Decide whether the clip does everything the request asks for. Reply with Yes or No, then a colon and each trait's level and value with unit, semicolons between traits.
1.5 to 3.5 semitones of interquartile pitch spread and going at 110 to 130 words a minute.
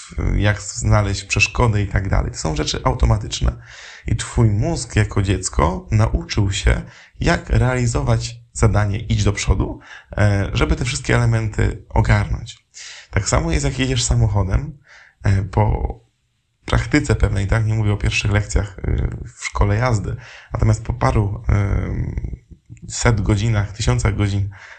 Yes: narrow, 2.5 semitones; average, 125 wpm